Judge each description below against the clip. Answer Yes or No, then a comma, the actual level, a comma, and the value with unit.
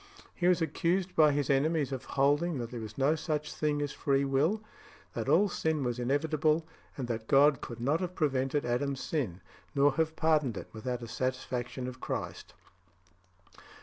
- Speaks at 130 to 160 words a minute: No, average, 175 wpm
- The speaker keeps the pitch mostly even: No, average, 3.6 semitones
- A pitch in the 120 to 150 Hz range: Yes, medium, 140 Hz